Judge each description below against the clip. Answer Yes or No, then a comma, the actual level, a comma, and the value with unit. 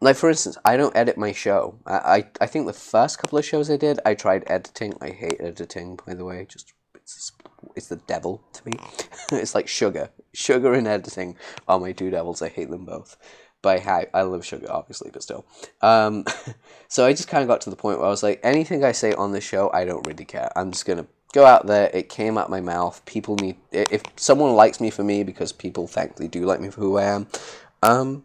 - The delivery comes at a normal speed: No, fast, 235 wpm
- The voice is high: No, low, 100 Hz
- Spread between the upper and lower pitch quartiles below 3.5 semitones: Yes, average, 2.9 semitones